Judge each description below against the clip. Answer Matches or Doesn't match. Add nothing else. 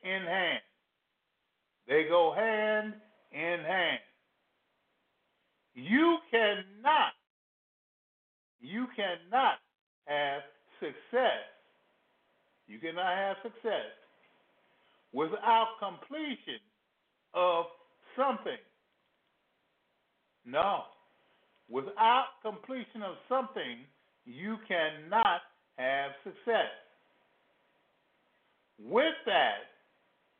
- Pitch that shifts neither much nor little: Doesn't match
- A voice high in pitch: Matches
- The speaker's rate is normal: Doesn't match